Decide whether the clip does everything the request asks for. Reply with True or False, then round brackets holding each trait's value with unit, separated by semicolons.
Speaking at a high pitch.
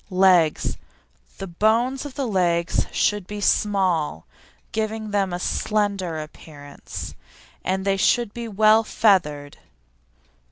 True (195 Hz)